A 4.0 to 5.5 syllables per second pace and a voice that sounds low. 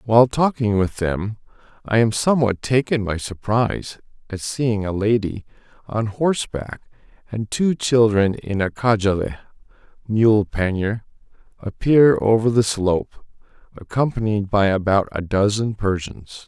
Yes: 4.5 syllables/s; low, 110 Hz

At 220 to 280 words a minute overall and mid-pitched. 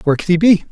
No: fast, 340 wpm; medium, 180 Hz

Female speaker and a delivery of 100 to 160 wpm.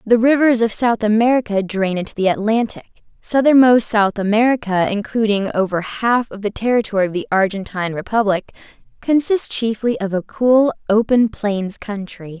Yes: female; average, 145 wpm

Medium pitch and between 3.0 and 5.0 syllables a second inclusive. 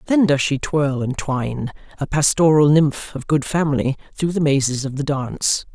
Yes: medium, 145 Hz; 4.9 syllables/s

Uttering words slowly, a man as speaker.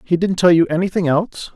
No: fast, 230 wpm; male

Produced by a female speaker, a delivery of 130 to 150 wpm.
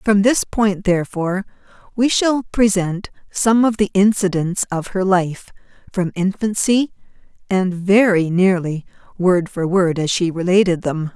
Yes: female; average, 140 wpm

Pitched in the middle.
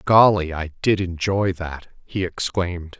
No: very low, 90 Hz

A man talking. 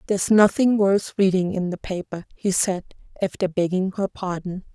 No: female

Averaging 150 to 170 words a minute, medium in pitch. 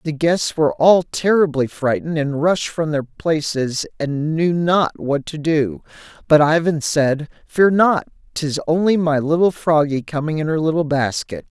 Yes: average, 165 wpm; medium, 155 Hz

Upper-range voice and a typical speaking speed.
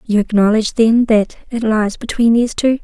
Yes: high, 225 Hz; average, 190 wpm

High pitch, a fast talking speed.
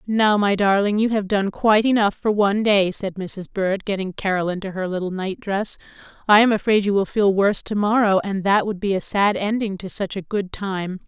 Yes: high, 200 Hz; fast, 225 wpm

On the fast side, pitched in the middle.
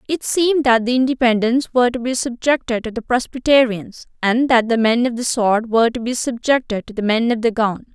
No: fast, 220 wpm; high, 240 Hz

